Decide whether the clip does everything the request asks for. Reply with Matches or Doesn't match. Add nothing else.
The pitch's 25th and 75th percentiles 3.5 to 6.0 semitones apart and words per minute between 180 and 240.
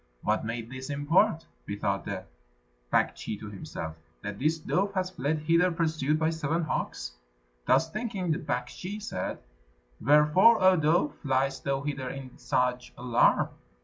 Doesn't match